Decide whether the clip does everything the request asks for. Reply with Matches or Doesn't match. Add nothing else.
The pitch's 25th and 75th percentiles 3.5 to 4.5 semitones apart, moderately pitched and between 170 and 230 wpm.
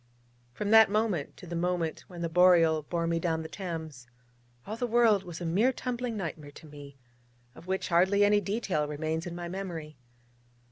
Matches